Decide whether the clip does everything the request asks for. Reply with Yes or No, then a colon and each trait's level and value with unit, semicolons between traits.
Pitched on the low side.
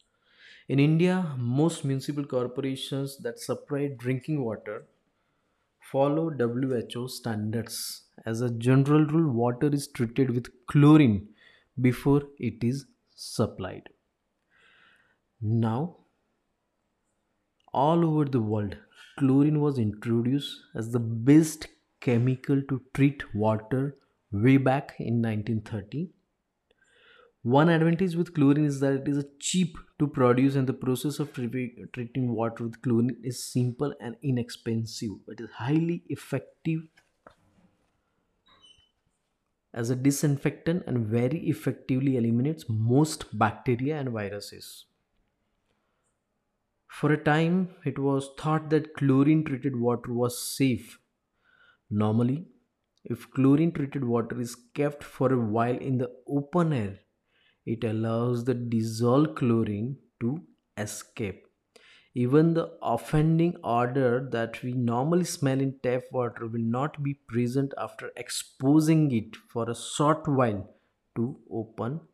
Yes: low, 130 Hz